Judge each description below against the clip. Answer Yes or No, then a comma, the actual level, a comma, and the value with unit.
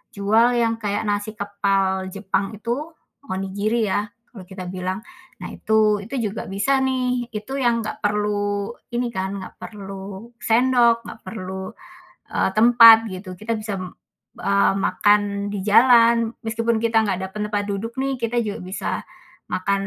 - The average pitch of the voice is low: No, high, 210 Hz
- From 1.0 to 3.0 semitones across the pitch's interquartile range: Yes, average, 2.7 semitones